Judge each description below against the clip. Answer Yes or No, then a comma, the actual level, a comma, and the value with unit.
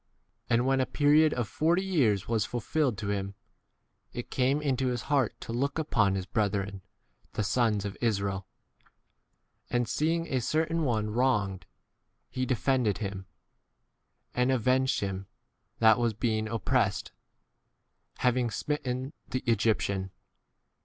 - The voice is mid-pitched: No, low, 120 Hz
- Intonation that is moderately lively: Yes, average, 4.2 semitones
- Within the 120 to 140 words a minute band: Yes, slow, 135 wpm